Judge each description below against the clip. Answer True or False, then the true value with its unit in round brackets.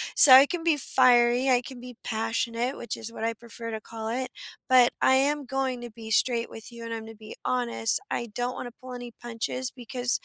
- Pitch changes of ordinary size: False (2.0 semitones)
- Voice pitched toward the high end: True (245 Hz)